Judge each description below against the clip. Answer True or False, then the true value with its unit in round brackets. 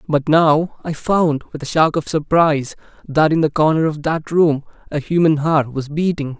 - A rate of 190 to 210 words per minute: True (195 wpm)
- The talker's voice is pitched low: False (155 Hz)